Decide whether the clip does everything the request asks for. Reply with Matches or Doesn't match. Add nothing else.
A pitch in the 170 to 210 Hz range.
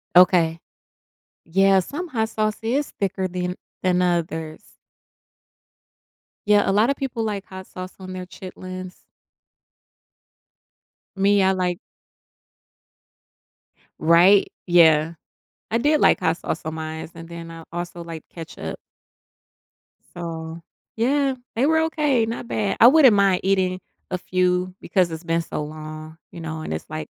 Matches